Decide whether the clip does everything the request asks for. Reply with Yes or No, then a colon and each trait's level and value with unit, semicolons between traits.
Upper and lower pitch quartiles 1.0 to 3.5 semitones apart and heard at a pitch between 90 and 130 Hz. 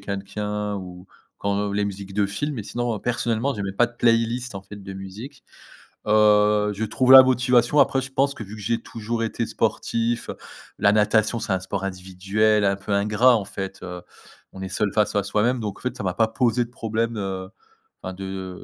Yes: average, 3.1 semitones; low, 105 Hz